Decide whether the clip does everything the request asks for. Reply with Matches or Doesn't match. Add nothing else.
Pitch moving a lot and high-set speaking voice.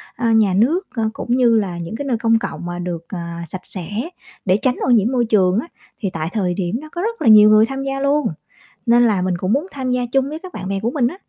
Matches